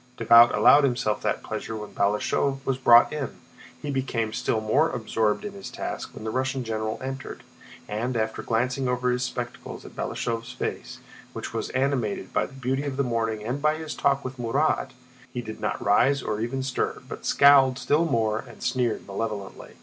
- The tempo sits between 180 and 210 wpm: Yes, average, 185 wpm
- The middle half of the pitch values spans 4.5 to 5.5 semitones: No, average, 3.3 semitones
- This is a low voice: Yes, low, 125 Hz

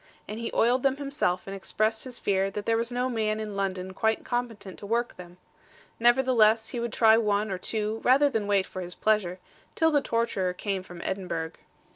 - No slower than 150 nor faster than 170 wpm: No, average, 200 wpm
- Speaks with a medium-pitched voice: No, high, 215 Hz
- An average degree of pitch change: Yes, average, 3.5 semitones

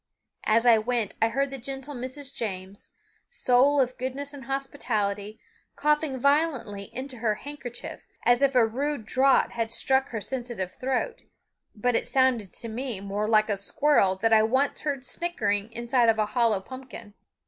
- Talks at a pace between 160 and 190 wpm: Yes, average, 165 wpm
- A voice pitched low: No, high, 245 Hz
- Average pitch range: Yes, average, 3.8 semitones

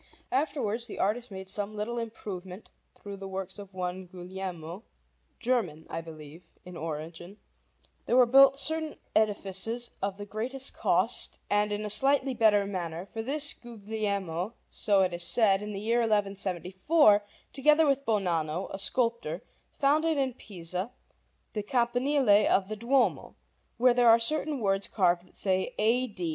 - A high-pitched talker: Yes, high, 210 Hz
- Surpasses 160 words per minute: No, average, 150 wpm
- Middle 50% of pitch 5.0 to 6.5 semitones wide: No, average, 4.3 semitones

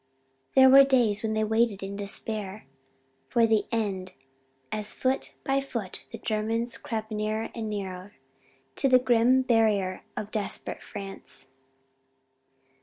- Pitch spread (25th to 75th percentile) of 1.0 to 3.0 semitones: Yes, narrow, 2.6 semitones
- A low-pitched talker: No, high, 220 Hz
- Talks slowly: Yes, slow, 130 wpm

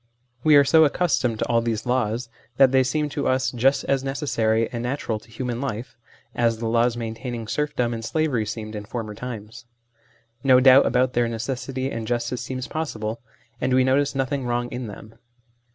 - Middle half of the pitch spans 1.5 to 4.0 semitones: Yes, average, 2.7 semitones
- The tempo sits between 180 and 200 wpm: Yes, average, 185 wpm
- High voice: No, low, 125 Hz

